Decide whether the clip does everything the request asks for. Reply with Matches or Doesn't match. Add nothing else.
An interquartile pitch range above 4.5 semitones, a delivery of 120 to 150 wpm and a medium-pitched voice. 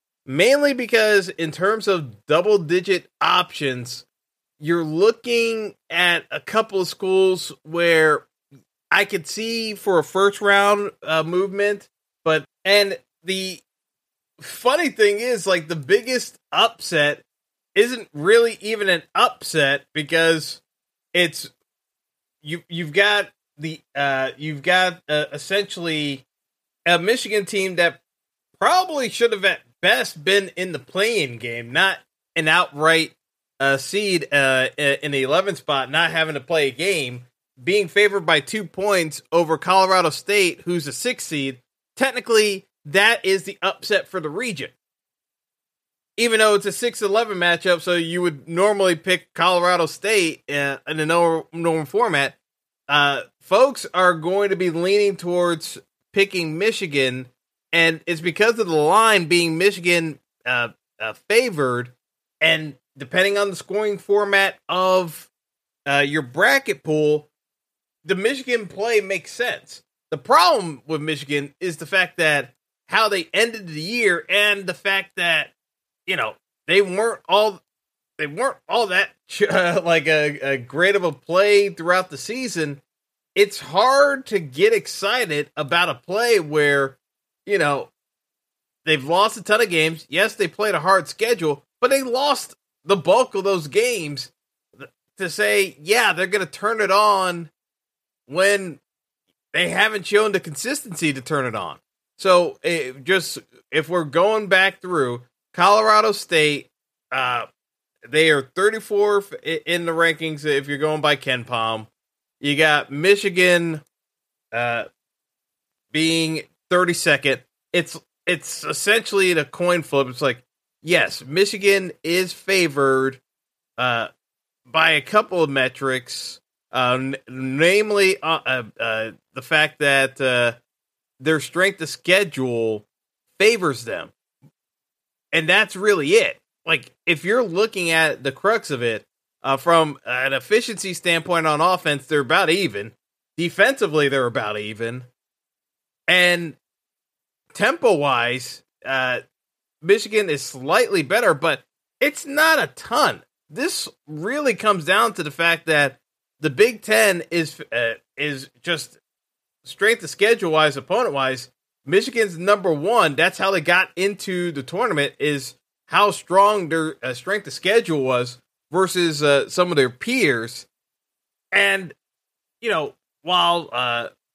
Matches